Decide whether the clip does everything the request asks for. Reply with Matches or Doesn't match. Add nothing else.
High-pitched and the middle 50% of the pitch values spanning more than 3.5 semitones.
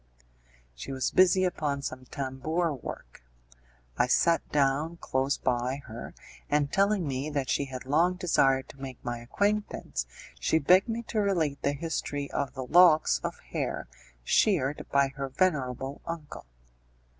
Doesn't match